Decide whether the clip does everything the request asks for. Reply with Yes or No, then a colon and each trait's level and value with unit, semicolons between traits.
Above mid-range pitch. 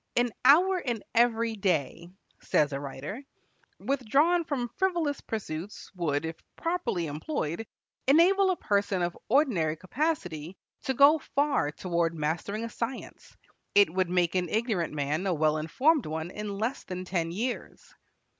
Yes: high, 200 Hz